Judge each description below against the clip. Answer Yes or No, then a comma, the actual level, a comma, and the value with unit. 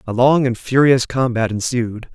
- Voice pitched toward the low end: Yes, low, 125 Hz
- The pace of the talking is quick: No, average, 170 wpm